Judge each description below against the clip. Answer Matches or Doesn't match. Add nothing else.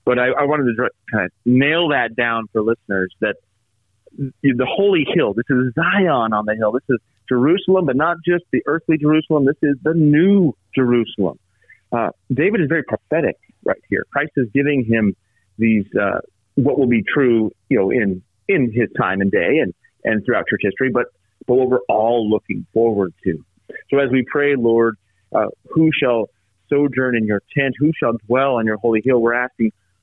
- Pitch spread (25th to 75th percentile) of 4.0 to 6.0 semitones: Matches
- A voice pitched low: Matches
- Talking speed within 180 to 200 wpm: Matches